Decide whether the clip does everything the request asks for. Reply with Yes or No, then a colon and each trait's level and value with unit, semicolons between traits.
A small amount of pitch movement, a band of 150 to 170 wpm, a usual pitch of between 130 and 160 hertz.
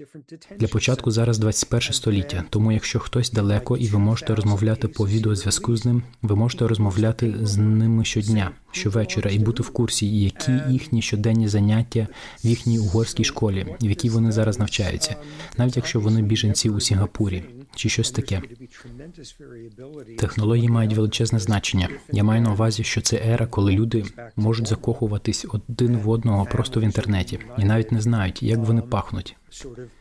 No: narrow, 1.6 semitones; fast, 155 wpm; low, 110 Hz